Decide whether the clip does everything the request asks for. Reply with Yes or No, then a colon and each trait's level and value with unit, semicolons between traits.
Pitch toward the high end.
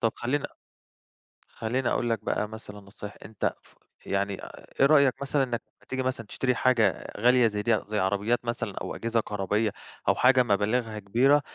No: low, 115 Hz